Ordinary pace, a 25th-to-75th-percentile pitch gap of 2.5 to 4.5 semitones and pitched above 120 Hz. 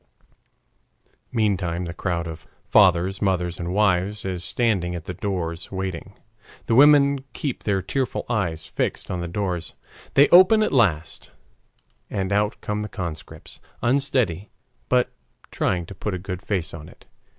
No: average, 150 wpm; average, 3.7 semitones; very low, 95 Hz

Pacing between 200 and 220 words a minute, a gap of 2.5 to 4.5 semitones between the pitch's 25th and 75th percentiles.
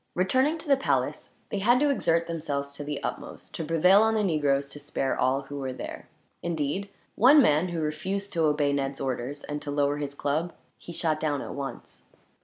No: fast, 205 wpm; average, 4.9 semitones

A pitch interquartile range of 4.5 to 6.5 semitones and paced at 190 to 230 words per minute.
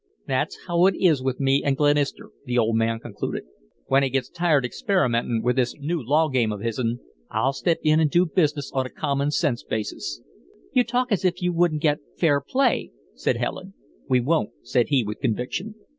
Yes: wide, 5.4 semitones; average, 195 wpm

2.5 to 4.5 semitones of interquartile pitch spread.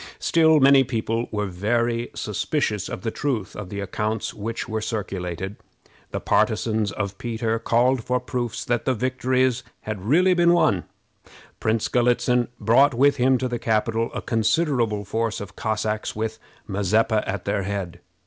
Yes: average, 3.1 semitones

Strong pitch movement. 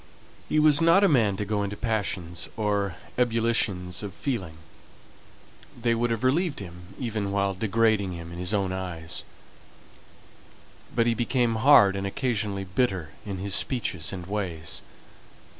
No: average, 4.0 semitones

